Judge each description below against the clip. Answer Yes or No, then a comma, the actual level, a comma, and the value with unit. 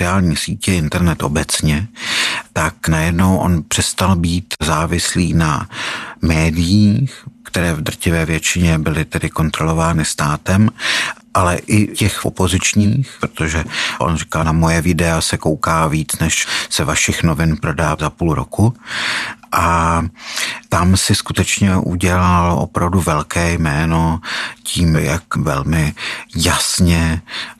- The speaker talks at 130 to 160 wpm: No, slow, 115 wpm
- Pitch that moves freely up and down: No, average, 2.7 semitones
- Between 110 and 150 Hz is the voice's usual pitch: No, very low, 85 Hz